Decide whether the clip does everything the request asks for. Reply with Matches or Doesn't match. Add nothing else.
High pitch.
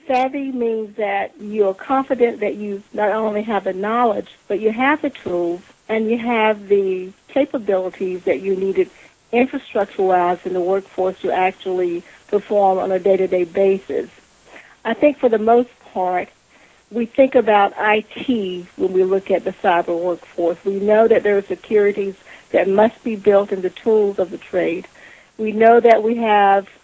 Matches